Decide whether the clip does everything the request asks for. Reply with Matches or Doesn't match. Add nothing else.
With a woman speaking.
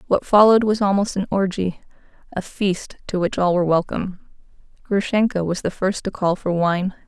Matches